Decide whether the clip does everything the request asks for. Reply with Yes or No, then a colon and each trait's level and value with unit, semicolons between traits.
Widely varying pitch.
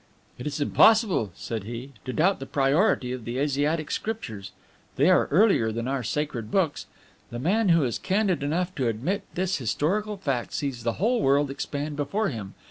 Yes: wide, 7.1 semitones